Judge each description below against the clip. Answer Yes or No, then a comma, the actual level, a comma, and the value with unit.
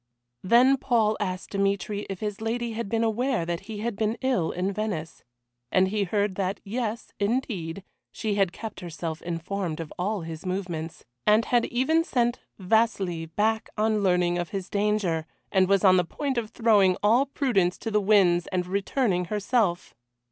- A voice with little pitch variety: No, average, 3.7 semitones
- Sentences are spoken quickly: No, average, 170 wpm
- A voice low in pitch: No, high, 200 Hz